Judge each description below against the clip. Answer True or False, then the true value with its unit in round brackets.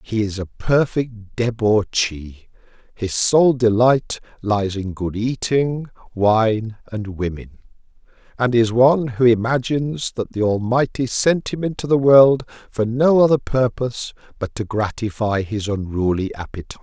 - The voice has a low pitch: True (115 Hz)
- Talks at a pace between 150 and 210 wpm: False (135 wpm)